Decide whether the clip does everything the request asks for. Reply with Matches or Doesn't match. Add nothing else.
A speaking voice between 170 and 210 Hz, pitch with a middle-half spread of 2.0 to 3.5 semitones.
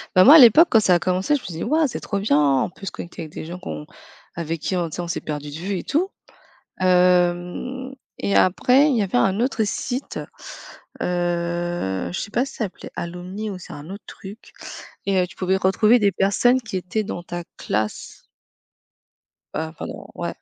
Doesn't match